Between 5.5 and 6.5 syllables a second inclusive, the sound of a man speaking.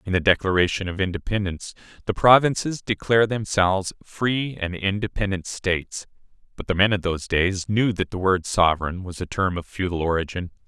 Yes: 5.6 syllables/s; male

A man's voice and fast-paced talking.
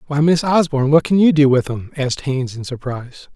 Yes: male; fast, 235 wpm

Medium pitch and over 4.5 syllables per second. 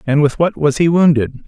Yes: medium, 150 Hz; 5.3 syllables/s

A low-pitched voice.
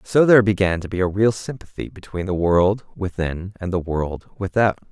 Yes: very low, 95 Hz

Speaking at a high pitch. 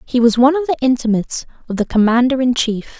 Yes: very high, 250 Hz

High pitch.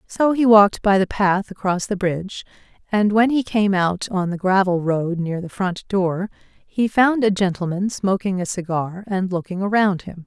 Yes: high, 195 Hz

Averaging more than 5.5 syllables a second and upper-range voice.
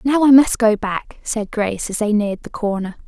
No: 5.2 syllables/s; high, 220 Hz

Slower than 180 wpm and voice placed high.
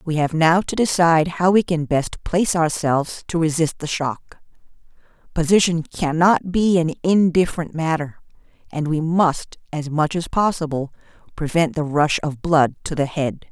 No: average, 160 wpm; medium, 160 Hz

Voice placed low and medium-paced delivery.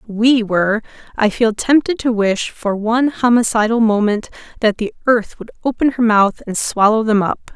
No: high, 225 Hz; average, 175 wpm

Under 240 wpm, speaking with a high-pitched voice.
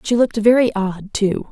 Yes: average, 200 wpm; high, 215 Hz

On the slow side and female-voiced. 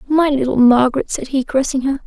No: fast, 205 wpm; female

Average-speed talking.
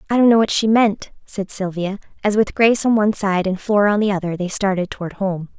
No: fast, 245 wpm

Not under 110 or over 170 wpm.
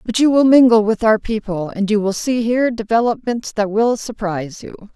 No: fast, 205 wpm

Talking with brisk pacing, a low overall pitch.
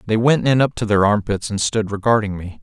Yes: fast, 250 wpm; low, 110 Hz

